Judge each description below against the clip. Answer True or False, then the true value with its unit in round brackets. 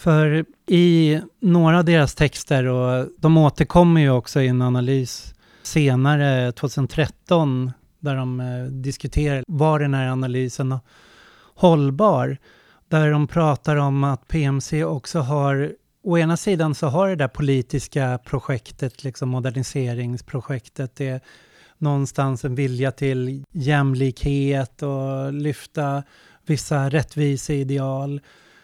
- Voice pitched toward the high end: False (140 Hz)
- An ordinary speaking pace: False (115 wpm)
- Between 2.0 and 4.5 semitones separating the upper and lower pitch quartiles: True (2.7 semitones)